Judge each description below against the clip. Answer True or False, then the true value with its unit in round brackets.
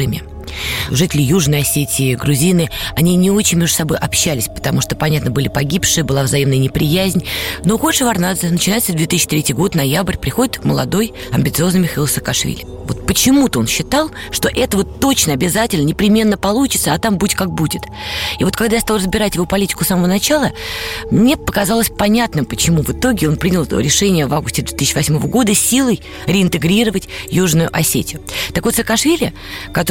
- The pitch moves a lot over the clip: True (5.9 semitones)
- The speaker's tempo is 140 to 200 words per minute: True (160 wpm)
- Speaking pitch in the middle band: True (175 Hz)